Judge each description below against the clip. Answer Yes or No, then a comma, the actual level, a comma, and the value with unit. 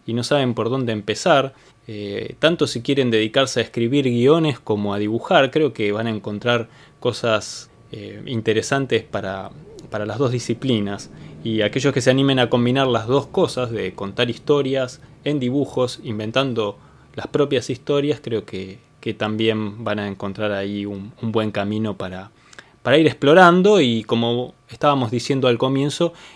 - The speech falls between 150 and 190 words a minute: Yes, average, 160 wpm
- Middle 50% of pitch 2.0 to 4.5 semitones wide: Yes, average, 4.1 semitones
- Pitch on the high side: No, low, 120 Hz